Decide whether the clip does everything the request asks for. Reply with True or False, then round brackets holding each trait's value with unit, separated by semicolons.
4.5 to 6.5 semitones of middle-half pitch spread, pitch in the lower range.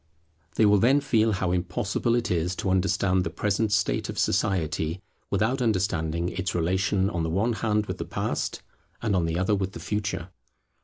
False (3.2 semitones; 95 Hz)